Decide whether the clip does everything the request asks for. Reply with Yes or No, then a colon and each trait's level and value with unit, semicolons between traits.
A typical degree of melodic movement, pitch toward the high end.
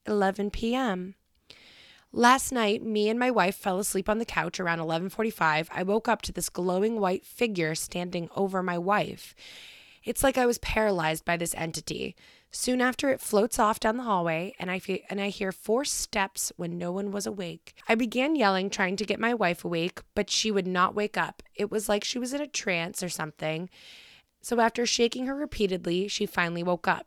Yes: average, 4.1 semitones; high, 200 Hz